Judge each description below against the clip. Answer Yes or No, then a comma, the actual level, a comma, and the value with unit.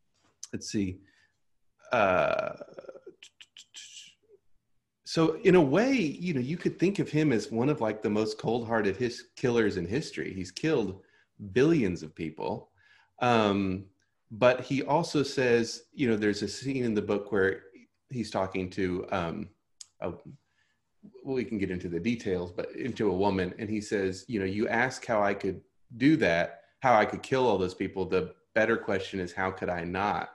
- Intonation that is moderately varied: No, wide, 6.3 semitones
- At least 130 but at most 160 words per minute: No, average, 180 wpm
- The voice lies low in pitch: Yes, low, 110 Hz